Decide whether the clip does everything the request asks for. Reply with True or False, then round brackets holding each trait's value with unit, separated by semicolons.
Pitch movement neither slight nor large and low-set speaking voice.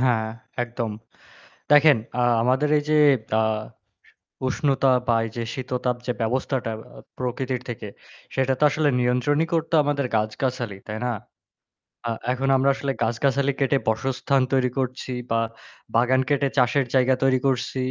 False (2.0 semitones; 130 Hz)